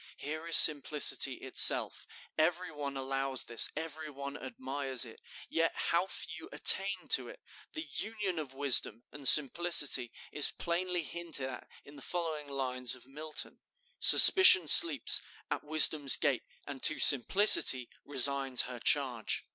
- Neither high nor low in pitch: Yes, medium, 145 Hz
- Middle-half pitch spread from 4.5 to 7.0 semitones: No, average, 3.7 semitones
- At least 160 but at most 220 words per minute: No, average, 140 wpm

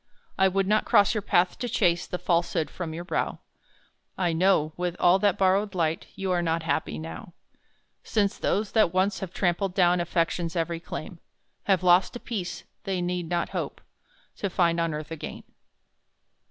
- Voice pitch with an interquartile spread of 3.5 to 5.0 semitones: No, narrow, 2.4 semitones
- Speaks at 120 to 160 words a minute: No, average, 175 wpm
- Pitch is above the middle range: No, medium, 180 Hz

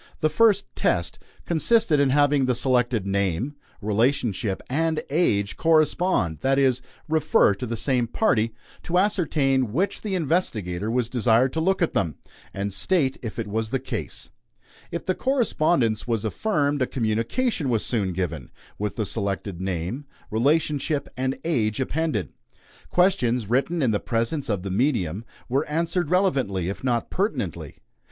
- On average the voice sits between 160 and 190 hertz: No, low, 130 Hz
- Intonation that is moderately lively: No, wide, 6.8 semitones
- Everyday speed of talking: Yes, average, 150 wpm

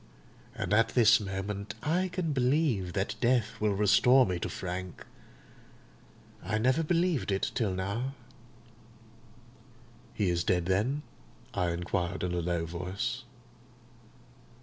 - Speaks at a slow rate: Yes, slow, 125 wpm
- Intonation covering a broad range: Yes, wide, 5.7 semitones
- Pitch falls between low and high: No, low, 105 Hz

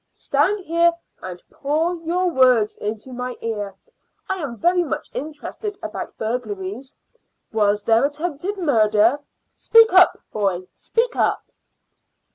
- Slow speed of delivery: Yes, slow, 120 wpm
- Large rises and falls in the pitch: Yes, wide, 8.3 semitones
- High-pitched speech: Yes, very high, 265 Hz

